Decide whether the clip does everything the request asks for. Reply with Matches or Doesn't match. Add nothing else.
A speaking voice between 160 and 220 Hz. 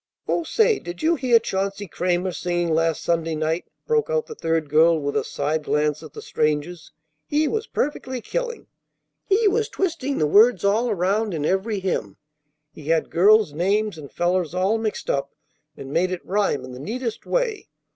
Matches